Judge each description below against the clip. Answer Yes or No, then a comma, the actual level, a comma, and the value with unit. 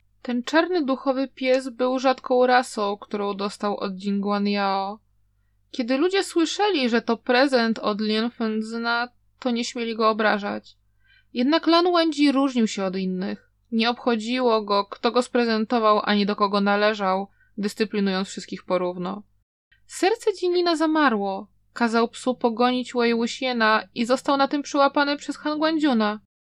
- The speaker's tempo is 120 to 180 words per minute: Yes, average, 135 wpm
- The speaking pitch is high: Yes, high, 235 Hz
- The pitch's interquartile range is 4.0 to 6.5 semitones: Yes, average, 4.5 semitones